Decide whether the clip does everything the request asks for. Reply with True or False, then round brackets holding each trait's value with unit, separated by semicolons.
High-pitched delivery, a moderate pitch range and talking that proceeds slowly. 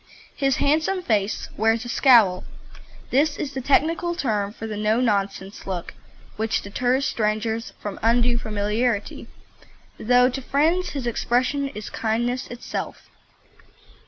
True (240 Hz; 4.2 semitones; 130 wpm)